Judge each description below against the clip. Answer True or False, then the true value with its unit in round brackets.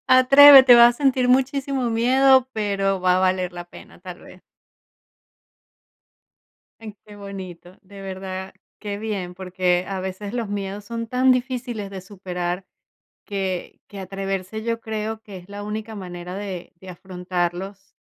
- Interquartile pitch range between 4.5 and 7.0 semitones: False (3.7 semitones)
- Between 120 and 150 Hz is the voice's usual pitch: False (200 Hz)